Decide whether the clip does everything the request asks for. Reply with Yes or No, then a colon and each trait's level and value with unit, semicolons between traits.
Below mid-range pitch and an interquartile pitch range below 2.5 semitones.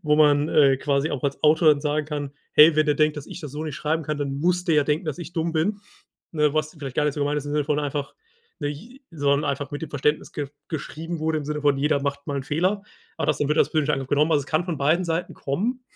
No: medium, 150 Hz; narrow, 1.8 semitones